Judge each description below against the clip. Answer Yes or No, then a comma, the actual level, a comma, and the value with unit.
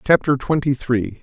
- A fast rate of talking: No, average, 145 wpm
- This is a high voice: No, low, 130 Hz